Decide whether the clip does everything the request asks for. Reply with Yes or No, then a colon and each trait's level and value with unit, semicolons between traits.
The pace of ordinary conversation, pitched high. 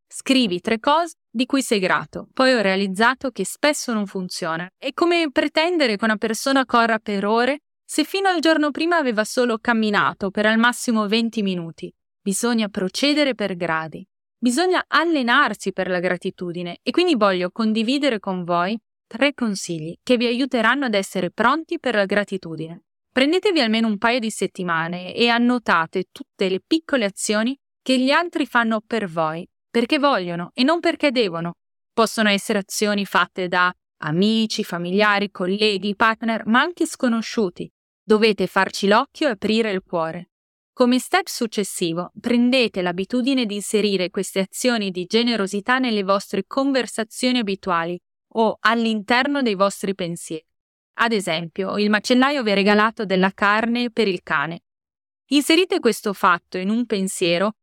Yes: average, 150 wpm; high, 220 Hz